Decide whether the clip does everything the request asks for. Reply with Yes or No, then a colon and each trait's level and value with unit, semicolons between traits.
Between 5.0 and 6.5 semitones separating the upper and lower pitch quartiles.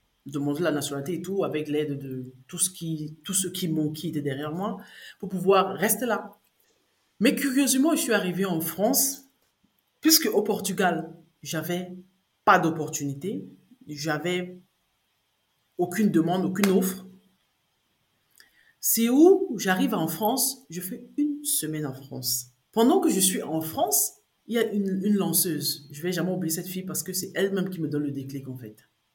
Yes: wide, 5.5 semitones